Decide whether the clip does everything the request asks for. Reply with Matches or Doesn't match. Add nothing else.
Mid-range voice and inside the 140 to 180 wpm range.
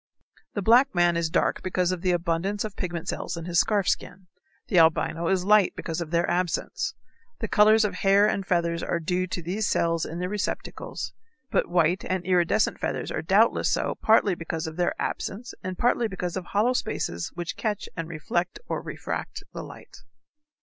Doesn't match